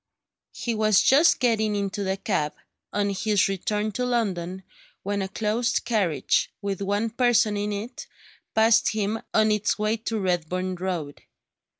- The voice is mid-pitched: No, high, 210 Hz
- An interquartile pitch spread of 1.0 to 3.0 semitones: Yes, narrow, 2.5 semitones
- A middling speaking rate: Yes, average, 150 wpm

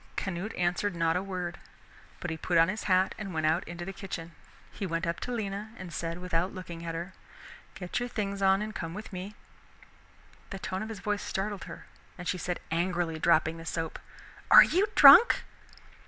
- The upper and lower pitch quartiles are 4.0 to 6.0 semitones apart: No, average, 2.8 semitones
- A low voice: No, medium, 180 Hz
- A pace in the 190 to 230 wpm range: Yes, average, 200 wpm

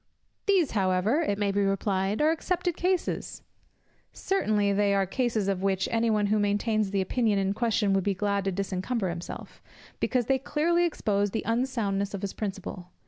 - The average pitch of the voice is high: Yes, high, 205 Hz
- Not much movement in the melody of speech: No, average, 3.6 semitones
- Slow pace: No, average, 175 wpm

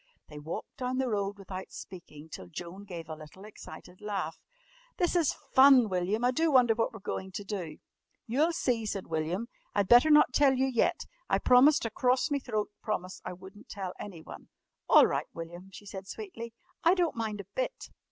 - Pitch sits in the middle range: No, high, 210 Hz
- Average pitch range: No, wide, 5.7 semitones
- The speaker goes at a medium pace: Yes, average, 190 wpm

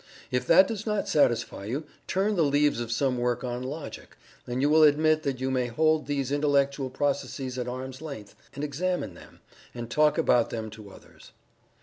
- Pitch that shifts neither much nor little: Yes, average, 3.7 semitones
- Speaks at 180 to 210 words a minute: Yes, average, 190 wpm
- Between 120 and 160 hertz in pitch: Yes, medium, 140 Hz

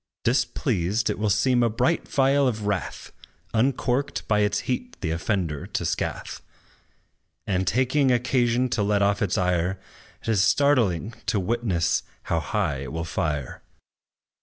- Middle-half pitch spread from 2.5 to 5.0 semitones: No, wide, 5.4 semitones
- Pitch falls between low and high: No, low, 105 Hz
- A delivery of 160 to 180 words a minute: No, average, 145 wpm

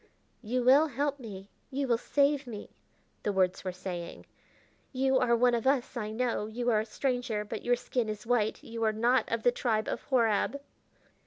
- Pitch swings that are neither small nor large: Yes, average, 3.0 semitones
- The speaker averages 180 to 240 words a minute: Yes, average, 190 wpm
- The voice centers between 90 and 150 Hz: No, high, 235 Hz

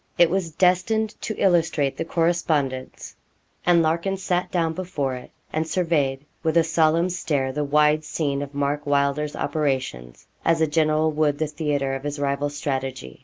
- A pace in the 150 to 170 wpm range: Yes, average, 165 wpm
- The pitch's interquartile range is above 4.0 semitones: No, average, 2.9 semitones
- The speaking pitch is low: No, medium, 155 Hz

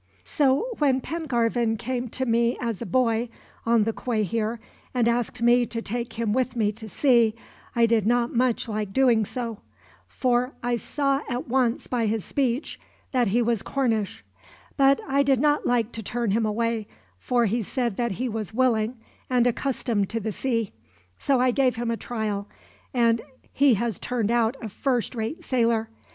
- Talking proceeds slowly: No, average, 180 wpm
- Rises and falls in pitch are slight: Yes, narrow, 2.3 semitones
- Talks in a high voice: Yes, high, 235 Hz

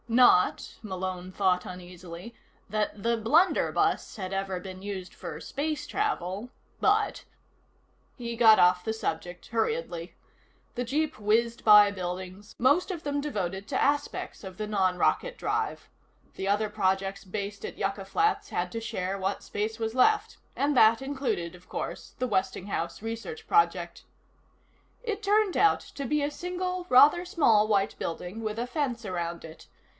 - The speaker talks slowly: No, average, 150 wpm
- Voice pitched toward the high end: Yes, high, 215 Hz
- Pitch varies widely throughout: Yes, wide, 7.2 semitones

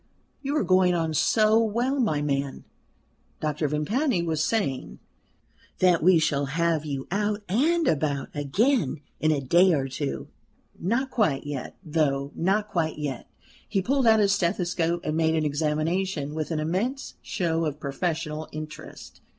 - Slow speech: No, average, 150 wpm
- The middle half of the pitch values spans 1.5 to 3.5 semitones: No, average, 5.2 semitones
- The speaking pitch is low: No, medium, 165 Hz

